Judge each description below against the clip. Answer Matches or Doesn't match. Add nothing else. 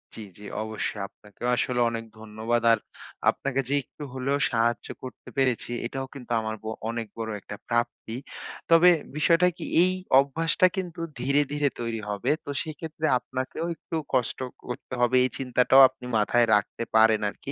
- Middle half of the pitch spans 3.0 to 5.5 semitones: Matches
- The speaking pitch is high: Doesn't match